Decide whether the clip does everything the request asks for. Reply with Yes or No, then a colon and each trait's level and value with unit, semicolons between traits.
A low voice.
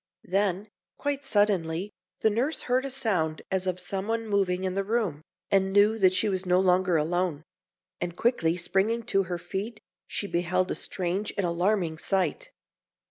No: high, 190 Hz